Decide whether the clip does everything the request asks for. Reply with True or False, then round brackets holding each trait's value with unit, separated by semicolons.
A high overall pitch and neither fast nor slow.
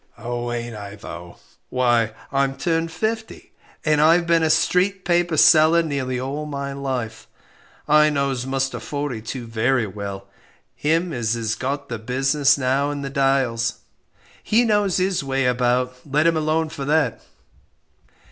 False (135 Hz; 150 wpm)